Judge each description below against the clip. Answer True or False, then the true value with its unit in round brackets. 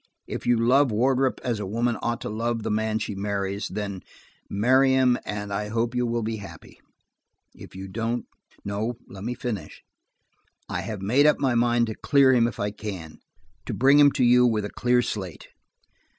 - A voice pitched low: True (115 Hz)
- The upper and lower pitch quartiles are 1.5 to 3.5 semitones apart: True (3.2 semitones)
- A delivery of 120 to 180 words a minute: False (190 wpm)